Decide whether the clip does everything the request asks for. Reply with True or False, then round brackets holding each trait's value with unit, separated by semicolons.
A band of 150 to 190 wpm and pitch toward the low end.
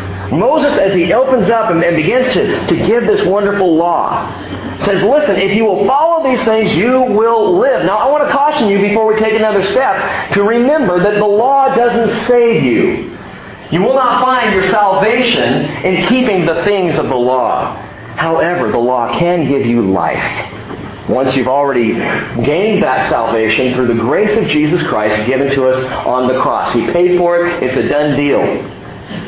False (180 wpm; 190 Hz)